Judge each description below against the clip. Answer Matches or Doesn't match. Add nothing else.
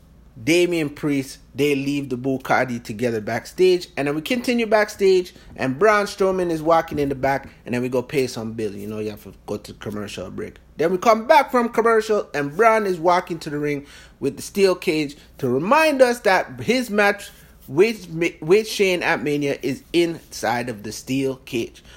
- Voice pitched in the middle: Matches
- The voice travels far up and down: Matches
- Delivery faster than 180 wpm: Matches